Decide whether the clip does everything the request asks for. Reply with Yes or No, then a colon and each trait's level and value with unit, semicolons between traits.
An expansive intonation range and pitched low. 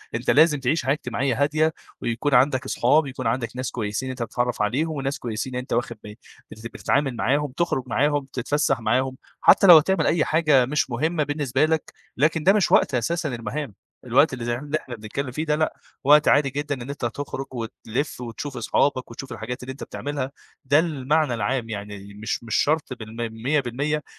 No: average, 3.7 semitones; low, 130 Hz